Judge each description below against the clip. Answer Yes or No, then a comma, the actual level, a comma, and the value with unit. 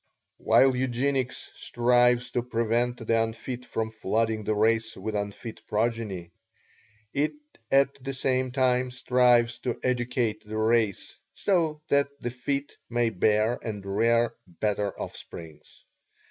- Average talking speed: No, slow, 125 wpm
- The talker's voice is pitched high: No, low, 120 Hz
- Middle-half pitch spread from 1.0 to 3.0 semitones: Yes, narrow, 2.5 semitones